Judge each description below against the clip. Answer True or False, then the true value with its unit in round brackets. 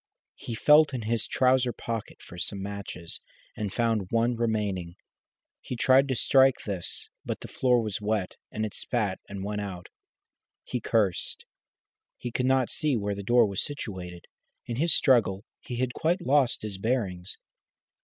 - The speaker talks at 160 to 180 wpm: True (165 wpm)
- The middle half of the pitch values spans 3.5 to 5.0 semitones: True (4.2 semitones)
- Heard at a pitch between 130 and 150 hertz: False (115 Hz)